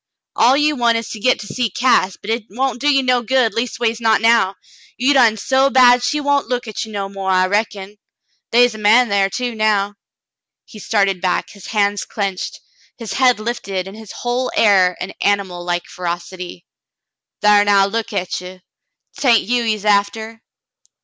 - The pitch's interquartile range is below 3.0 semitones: No, average, 3.7 semitones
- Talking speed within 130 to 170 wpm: No, average, 185 wpm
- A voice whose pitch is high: Yes, high, 220 Hz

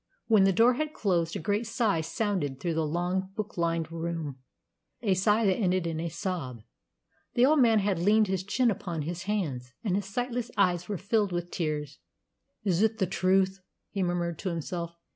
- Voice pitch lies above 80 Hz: Yes, medium, 185 Hz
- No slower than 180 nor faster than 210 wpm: Yes, average, 190 wpm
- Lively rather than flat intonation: No, average, 3.7 semitones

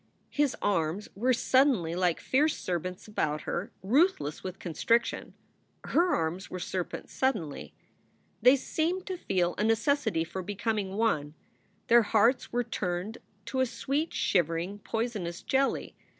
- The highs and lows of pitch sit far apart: Yes, wide, 6.6 semitones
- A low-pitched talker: No, high, 210 Hz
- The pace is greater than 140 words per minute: No, slow, 135 wpm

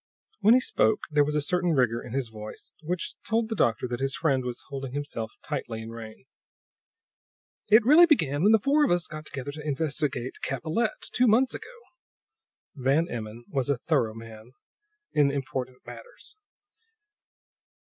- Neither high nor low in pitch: Yes, medium, 145 Hz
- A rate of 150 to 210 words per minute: Yes, average, 165 wpm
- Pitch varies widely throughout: Yes, wide, 6.6 semitones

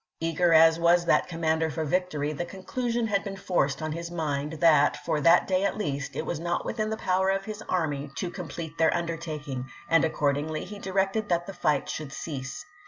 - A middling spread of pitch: Yes, average, 3.5 semitones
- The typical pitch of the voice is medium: Yes, medium, 165 Hz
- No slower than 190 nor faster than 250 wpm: Yes, average, 200 wpm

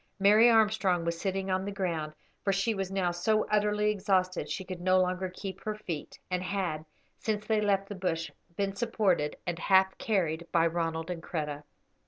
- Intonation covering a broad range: No, average, 2.9 semitones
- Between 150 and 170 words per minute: No, average, 185 wpm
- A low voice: No, high, 190 Hz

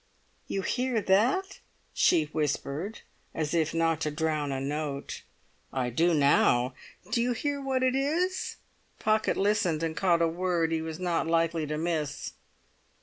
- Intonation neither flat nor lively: No, wide, 5.9 semitones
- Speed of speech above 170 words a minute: No, average, 150 wpm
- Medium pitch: Yes, medium, 165 Hz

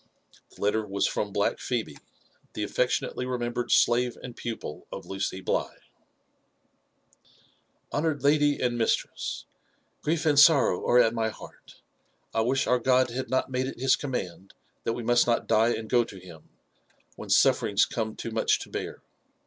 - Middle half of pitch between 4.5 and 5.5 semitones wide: No, average, 2.8 semitones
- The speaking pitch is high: No, low, 120 Hz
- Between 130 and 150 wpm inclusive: No, average, 165 wpm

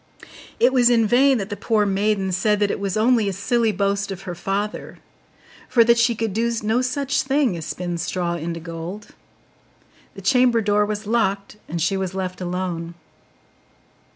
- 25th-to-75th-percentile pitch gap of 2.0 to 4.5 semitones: Yes, average, 4.0 semitones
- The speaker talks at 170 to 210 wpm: Yes, average, 180 wpm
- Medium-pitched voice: No, high, 205 Hz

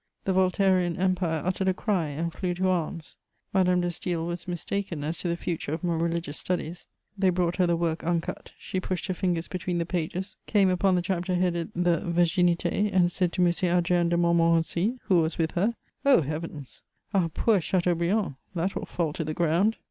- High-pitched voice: No, medium, 175 Hz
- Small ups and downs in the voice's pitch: Yes, narrow, 1.7 semitones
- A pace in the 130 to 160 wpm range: No, average, 195 wpm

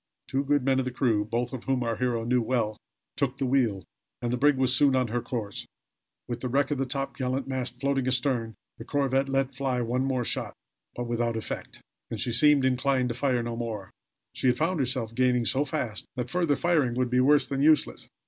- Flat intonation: Yes, narrow, 2.2 semitones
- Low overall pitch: Yes, low, 130 Hz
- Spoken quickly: Yes, fast, 215 wpm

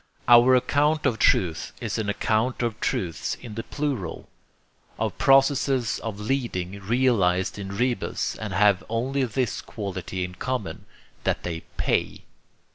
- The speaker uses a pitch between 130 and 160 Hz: No, low, 110 Hz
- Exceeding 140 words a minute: No, slow, 135 wpm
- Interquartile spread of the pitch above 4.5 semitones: Yes, average, 5.0 semitones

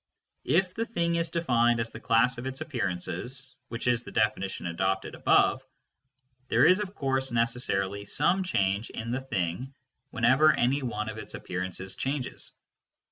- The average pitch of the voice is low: Yes, low, 120 Hz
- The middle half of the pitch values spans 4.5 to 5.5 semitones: Yes, average, 5.2 semitones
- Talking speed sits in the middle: Yes, average, 155 wpm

